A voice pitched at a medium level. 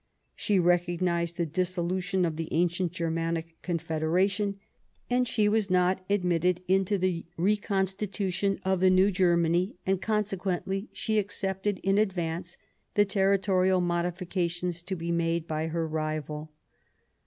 Yes: medium, 180 Hz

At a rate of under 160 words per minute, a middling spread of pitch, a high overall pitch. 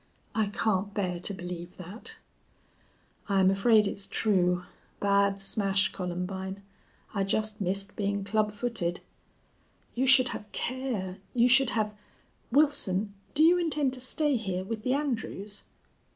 Yes: slow, 135 wpm; average, 4.0 semitones; high, 205 Hz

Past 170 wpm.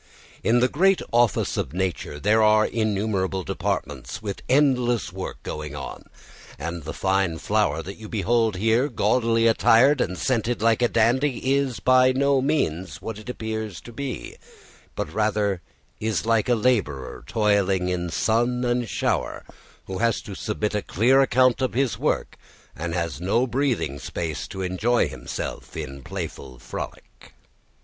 No: average, 155 wpm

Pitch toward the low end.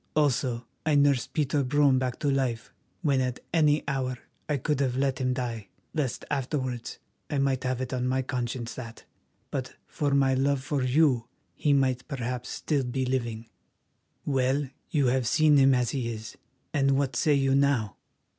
Yes: low, 130 Hz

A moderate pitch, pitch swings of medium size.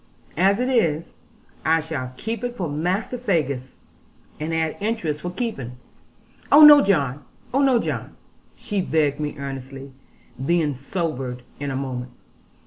No: medium, 160 Hz; wide, 6.6 semitones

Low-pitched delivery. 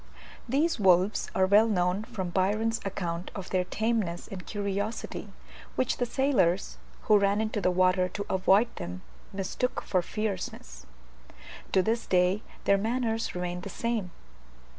No: high, 195 Hz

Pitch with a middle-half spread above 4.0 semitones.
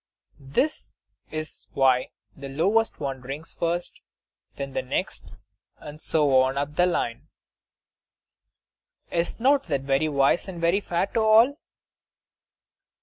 Yes: average, 4.9 semitones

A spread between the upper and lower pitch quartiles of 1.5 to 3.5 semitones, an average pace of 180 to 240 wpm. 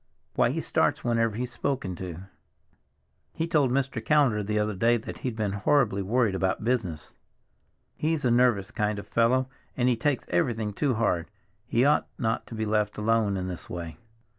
No: average, 3.9 semitones; average, 185 wpm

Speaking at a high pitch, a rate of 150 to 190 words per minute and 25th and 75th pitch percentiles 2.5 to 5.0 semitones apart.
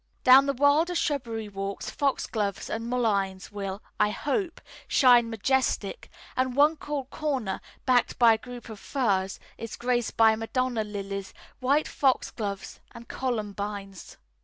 No: high, 235 Hz; slow, 135 wpm; average, 4.5 semitones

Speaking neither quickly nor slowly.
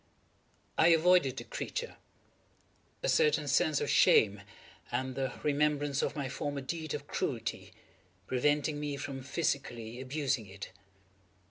No: slow, 125 wpm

